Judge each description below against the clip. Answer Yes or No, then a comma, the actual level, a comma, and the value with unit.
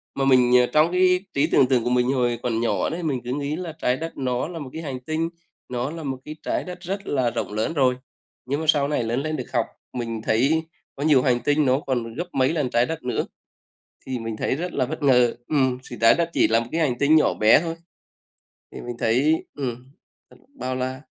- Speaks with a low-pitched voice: Yes, low, 130 Hz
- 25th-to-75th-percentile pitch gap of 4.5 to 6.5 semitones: No, average, 4.1 semitones